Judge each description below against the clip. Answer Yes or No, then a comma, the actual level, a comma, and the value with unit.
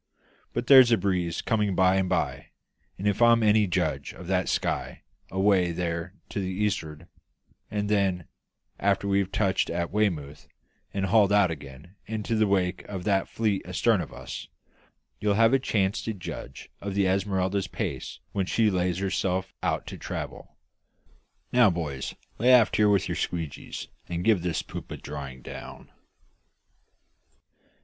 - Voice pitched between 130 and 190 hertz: No, very low, 95 Hz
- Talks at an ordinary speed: Yes, average, 155 wpm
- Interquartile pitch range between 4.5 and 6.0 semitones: No, average, 2.8 semitones